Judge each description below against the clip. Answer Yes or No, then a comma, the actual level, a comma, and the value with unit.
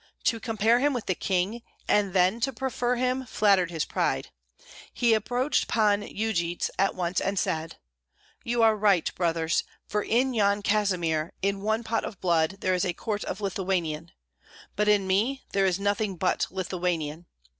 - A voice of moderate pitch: No, high, 200 Hz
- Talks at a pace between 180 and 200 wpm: No, average, 165 wpm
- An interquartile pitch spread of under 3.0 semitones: No, average, 3.8 semitones